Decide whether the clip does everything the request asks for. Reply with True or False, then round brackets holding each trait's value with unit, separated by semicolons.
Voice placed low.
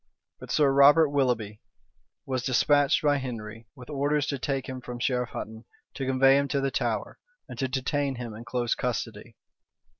True (130 Hz)